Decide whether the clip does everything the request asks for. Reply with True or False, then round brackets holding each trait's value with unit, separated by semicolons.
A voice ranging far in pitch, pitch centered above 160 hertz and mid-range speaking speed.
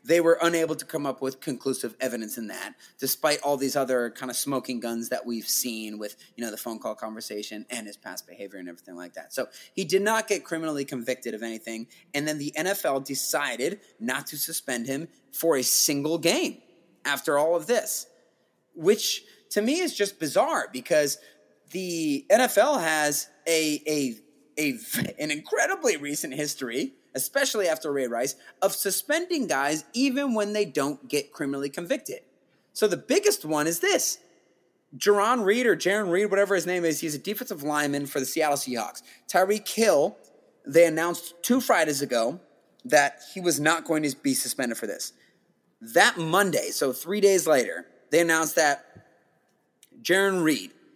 False (6.6 semitones; 155 Hz; 170 wpm)